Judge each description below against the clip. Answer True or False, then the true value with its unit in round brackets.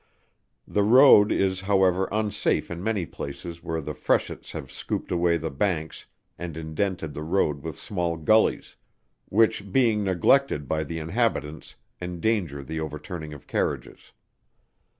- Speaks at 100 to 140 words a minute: True (135 wpm)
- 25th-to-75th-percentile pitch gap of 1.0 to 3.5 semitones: False (4.5 semitones)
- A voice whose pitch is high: False (85 Hz)